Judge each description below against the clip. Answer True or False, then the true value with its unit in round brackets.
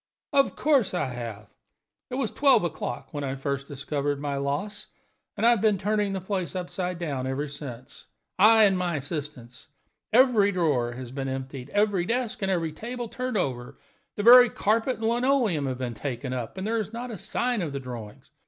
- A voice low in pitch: False (175 Hz)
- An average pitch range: False (8.3 semitones)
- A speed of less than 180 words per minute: False (190 wpm)